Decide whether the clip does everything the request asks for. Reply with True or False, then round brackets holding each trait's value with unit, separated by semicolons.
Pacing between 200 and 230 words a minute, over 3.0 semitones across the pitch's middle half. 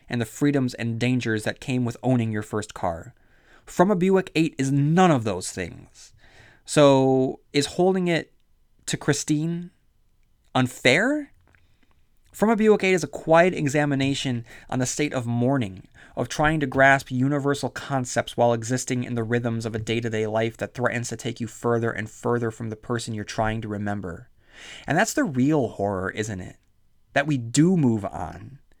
False (175 wpm; 4.3 semitones)